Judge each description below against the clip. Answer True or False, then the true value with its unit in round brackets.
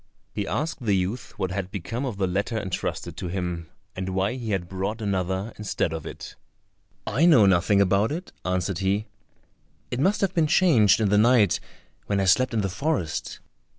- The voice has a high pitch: False (100 Hz)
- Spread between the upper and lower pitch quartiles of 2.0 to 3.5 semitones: False (3.9 semitones)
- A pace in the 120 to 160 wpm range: False (185 wpm)